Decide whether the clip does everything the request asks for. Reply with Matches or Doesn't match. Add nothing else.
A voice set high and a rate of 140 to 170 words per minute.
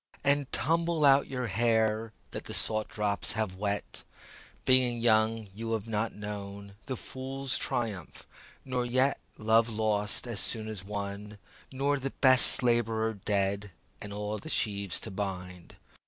Doesn't match